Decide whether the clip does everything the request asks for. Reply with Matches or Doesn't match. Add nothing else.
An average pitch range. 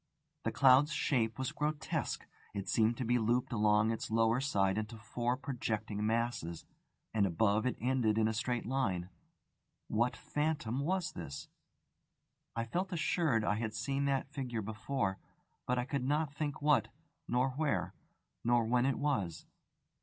Matches